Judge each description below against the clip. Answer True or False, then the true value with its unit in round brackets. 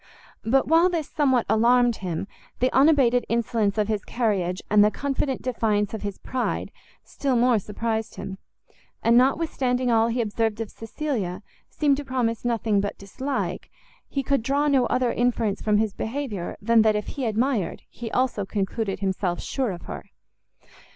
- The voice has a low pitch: False (230 Hz)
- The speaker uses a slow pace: False (165 wpm)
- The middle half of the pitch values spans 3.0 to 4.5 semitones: True (3.7 semitones)